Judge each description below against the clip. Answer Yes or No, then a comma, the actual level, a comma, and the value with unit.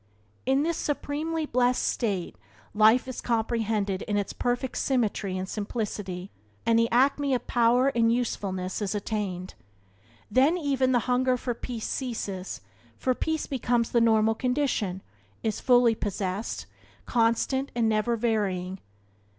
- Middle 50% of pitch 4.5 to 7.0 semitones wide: No, average, 3.6 semitones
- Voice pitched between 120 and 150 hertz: No, high, 230 Hz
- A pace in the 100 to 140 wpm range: Yes, slow, 135 wpm